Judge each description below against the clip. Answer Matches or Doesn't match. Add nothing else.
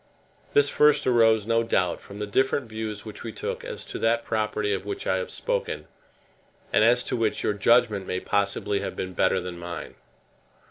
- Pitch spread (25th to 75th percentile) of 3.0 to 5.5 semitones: Doesn't match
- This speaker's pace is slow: Doesn't match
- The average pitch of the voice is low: Matches